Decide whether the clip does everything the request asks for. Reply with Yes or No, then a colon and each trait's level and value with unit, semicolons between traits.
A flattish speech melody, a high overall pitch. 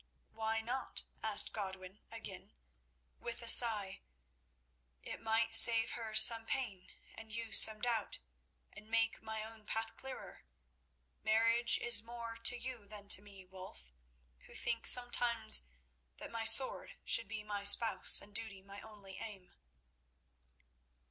Yes: narrow, 2.1 semitones; high, 220 Hz